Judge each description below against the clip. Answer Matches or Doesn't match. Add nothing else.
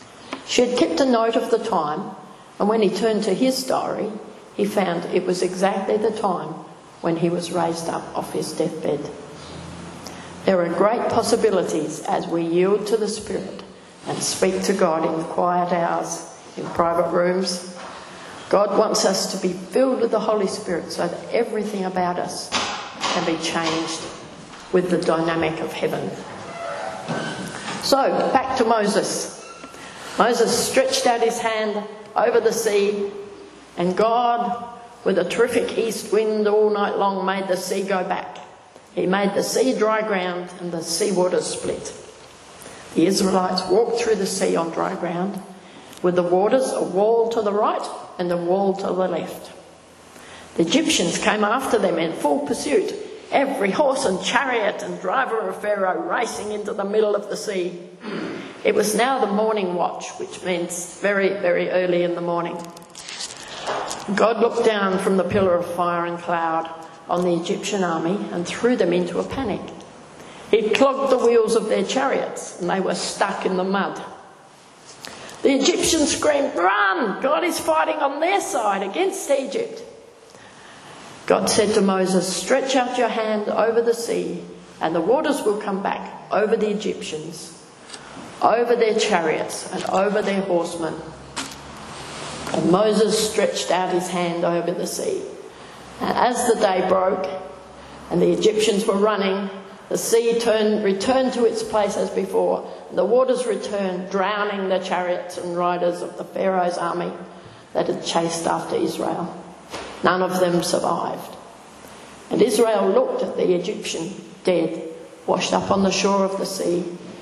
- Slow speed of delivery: Doesn't match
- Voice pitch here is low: Doesn't match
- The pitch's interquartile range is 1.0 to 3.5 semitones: Doesn't match